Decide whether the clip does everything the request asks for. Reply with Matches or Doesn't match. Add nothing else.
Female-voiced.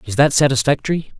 Doesn't match